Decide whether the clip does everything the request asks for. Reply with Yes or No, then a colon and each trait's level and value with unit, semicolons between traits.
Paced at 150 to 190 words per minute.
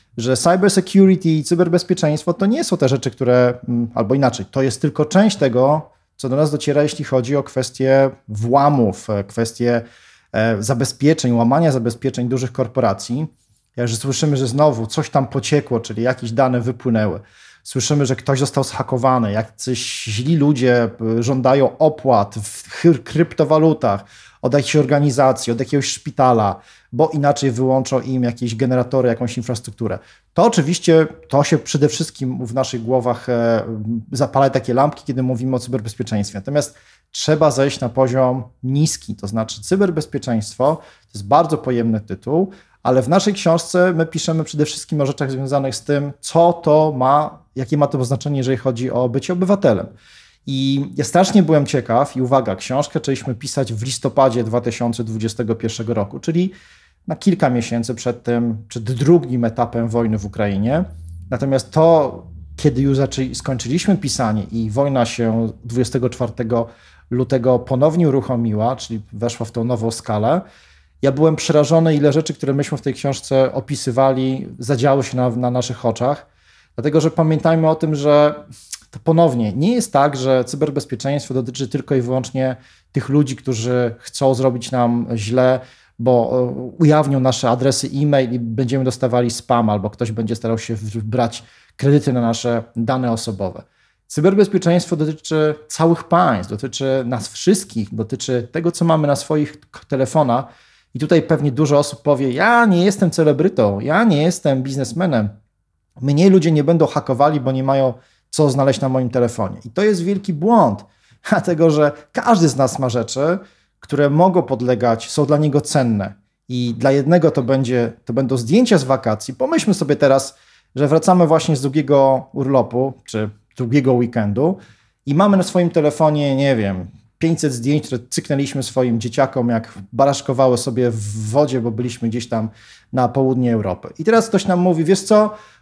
Yes: average, 155 wpm